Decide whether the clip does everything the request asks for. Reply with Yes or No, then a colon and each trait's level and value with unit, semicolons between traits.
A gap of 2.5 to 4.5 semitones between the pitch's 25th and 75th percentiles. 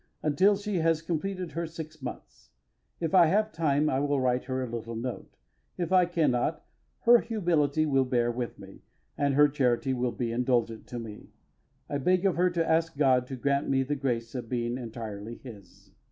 No: average, 5.0 semitones